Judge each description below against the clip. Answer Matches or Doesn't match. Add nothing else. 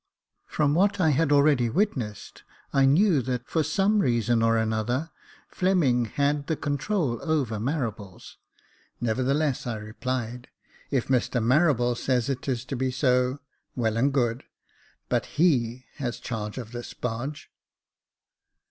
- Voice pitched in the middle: Doesn't match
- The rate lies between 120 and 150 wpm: Matches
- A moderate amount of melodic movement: Matches